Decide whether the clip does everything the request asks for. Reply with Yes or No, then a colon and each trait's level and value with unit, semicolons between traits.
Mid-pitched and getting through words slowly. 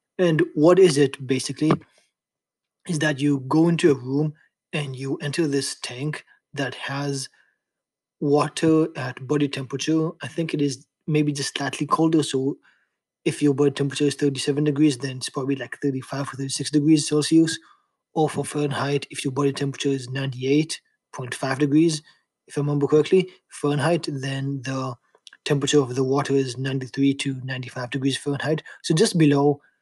No: medium, 145 Hz; average, 155 wpm